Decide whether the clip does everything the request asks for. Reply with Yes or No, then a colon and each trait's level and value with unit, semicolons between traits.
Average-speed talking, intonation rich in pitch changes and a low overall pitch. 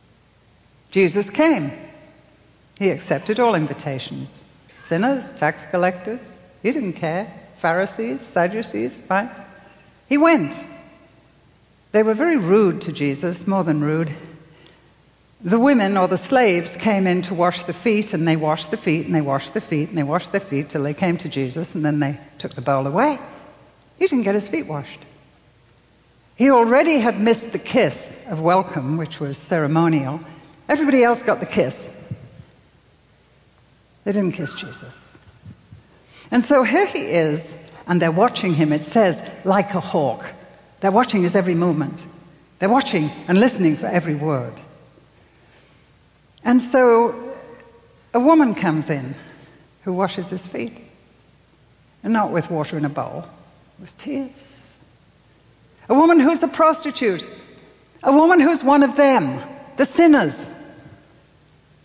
No: average, 145 wpm; wide, 7.1 semitones; medium, 180 Hz